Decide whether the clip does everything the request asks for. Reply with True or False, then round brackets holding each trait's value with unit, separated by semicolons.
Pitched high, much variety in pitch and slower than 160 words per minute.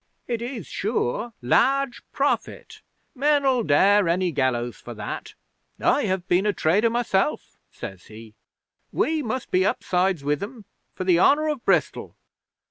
True (195 Hz; 7.6 semitones; 140 wpm)